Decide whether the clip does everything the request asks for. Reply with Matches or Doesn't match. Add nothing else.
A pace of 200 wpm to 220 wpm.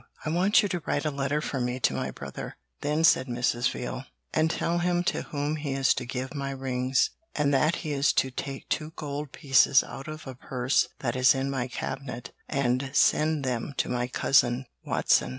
Matches